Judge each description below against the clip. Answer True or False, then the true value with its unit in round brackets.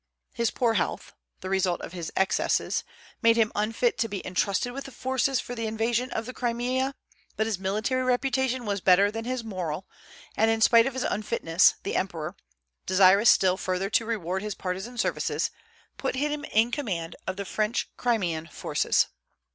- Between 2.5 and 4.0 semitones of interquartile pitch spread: False (4.4 semitones)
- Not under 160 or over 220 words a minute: True (175 wpm)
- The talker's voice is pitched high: True (220 Hz)